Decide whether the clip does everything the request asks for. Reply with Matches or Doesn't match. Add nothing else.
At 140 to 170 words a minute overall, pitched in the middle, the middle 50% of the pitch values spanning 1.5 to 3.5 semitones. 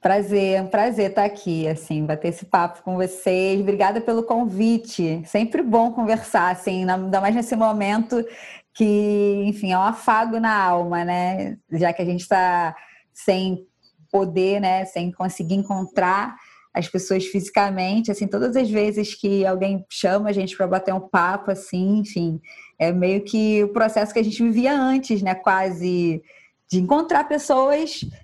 Doesn't match